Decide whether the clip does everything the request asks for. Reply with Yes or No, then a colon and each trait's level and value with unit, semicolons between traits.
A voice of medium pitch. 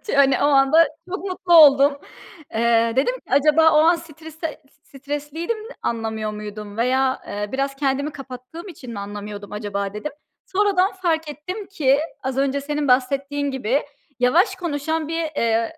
No: very high, 280 Hz